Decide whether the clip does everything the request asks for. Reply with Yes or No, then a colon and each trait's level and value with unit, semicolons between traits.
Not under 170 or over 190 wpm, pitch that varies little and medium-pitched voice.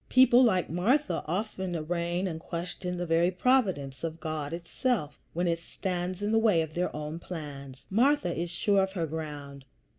No: average, 175 wpm; average, 3.3 semitones; medium, 175 Hz